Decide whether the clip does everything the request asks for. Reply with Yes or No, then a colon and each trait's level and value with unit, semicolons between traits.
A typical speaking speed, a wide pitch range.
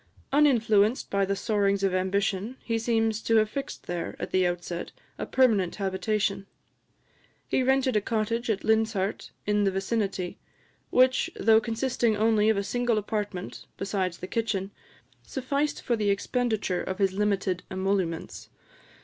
No: average, 145 wpm; average, 2.9 semitones